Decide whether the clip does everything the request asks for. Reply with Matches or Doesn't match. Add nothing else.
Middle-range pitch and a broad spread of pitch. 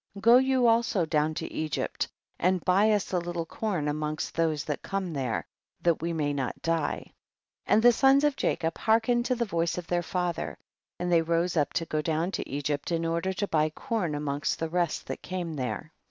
Doesn't match